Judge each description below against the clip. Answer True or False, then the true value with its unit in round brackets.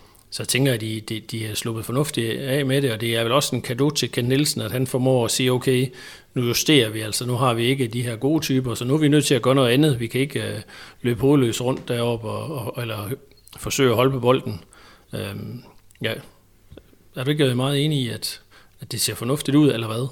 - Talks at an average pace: False (245 wpm)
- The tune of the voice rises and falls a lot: False (3.0 semitones)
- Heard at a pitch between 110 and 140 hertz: True (125 Hz)